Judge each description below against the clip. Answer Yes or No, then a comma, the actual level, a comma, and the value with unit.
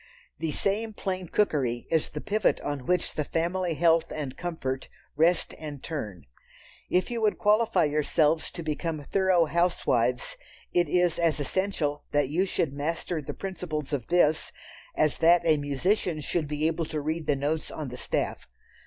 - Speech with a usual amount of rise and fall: Yes, average, 3.4 semitones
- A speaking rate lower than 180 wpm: Yes, average, 165 wpm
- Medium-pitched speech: Yes, medium, 160 Hz